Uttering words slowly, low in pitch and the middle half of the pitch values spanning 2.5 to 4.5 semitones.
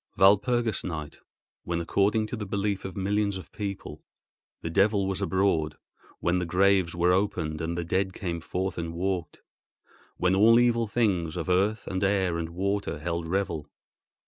No: average, 160 wpm; very low, 95 Hz; average, 3.0 semitones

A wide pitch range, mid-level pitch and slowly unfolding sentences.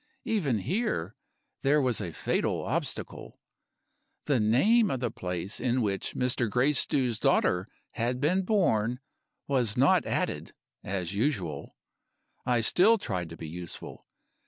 No: wide, 6.8 semitones; low, 120 Hz; slow, 130 wpm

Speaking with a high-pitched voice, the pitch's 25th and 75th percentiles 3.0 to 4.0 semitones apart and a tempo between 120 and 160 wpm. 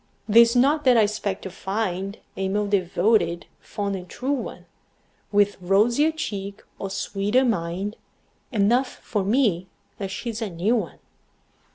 Yes: high, 205 Hz; average, 3.4 semitones; average, 145 wpm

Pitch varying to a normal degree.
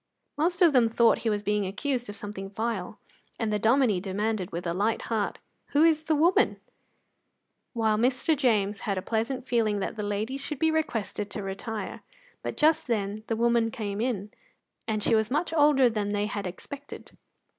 Yes: average, 4.2 semitones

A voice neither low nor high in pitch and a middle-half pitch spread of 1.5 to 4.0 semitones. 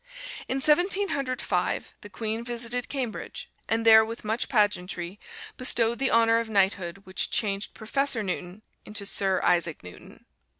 No: high, 220 Hz; average, 3.5 semitones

